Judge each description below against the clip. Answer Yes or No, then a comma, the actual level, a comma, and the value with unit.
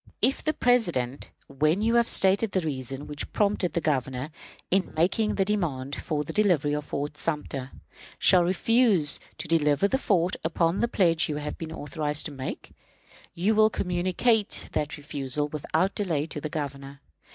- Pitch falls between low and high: Yes, medium, 160 Hz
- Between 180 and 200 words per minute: No, average, 165 wpm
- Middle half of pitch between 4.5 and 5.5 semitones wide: Yes, average, 5.1 semitones